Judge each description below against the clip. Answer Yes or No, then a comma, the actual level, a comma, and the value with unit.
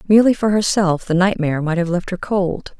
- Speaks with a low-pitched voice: No, medium, 185 Hz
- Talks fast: Yes, fast, 215 wpm